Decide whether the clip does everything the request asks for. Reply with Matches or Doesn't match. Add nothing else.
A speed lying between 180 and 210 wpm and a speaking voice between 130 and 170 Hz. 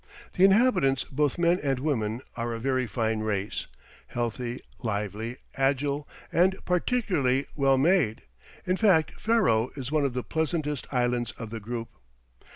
Doesn't match